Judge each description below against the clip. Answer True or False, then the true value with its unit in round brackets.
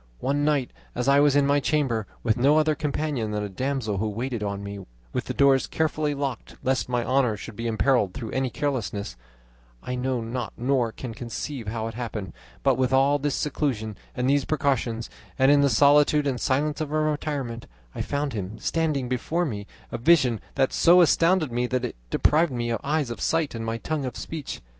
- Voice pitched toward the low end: True (130 Hz)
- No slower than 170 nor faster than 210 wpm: True (200 wpm)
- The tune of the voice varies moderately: True (3.9 semitones)